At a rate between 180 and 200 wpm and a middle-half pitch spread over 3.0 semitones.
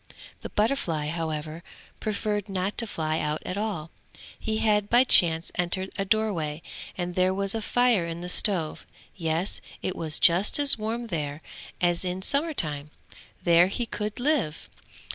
No: average, 160 wpm; average, 4.7 semitones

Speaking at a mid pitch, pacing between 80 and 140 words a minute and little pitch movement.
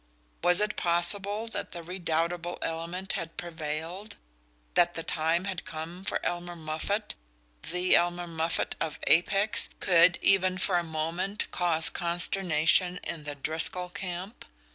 Yes: medium, 175 Hz; slow, 135 wpm; narrow, 2.1 semitones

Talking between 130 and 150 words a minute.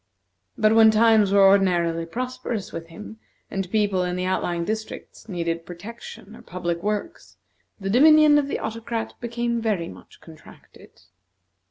Yes: average, 145 wpm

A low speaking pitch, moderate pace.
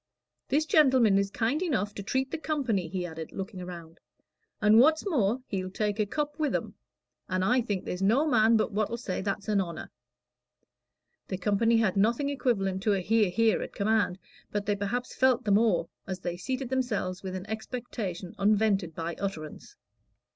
No: high, 210 Hz; average, 180 wpm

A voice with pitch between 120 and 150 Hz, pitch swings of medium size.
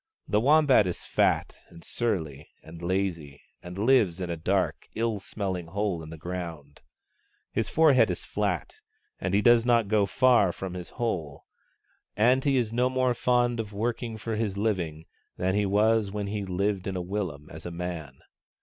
No: low, 100 Hz; average, 4.7 semitones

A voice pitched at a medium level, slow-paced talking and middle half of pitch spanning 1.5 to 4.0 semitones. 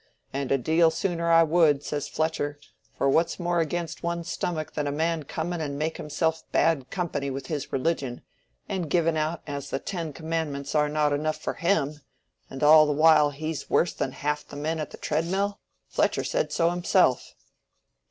No: medium, 155 Hz; average, 185 wpm; narrow, 2.4 semitones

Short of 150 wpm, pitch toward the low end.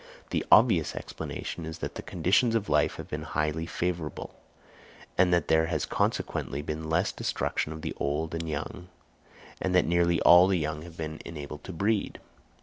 No: average, 175 wpm; very low, 80 Hz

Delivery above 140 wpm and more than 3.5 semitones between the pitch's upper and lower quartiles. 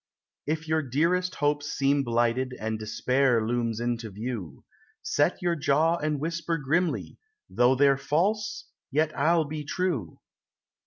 No: slow, 135 wpm; average, 4.9 semitones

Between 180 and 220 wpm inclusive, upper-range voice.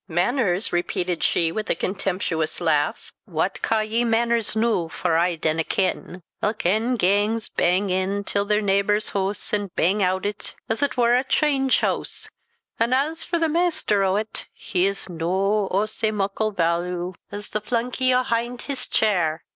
No: average, 165 wpm; high, 205 Hz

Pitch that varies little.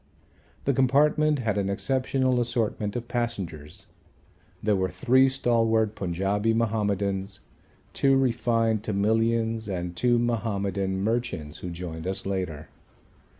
No: average, 3.8 semitones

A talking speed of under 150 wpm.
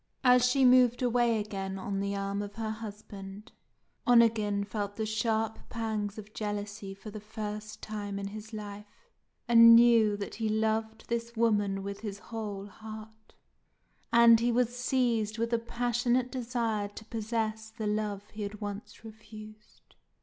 No: average, 155 wpm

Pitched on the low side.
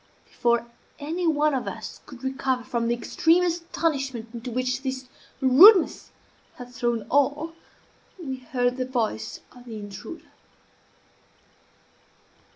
No: very high, 260 Hz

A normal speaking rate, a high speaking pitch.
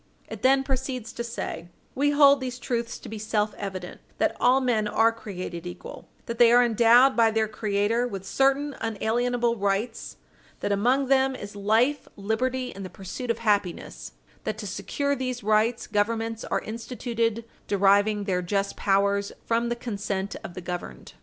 Yes: average, 165 wpm; high, 225 Hz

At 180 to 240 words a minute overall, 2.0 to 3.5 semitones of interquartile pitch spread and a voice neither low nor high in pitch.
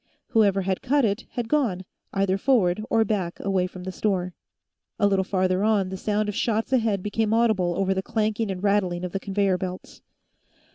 No: average, 190 wpm; average, 2.7 semitones; high, 200 Hz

